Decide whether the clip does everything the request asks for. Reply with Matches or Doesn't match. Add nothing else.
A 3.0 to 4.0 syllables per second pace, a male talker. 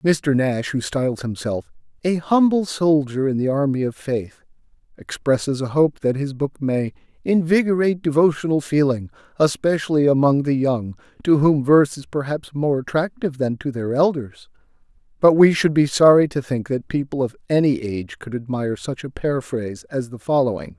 Doesn't match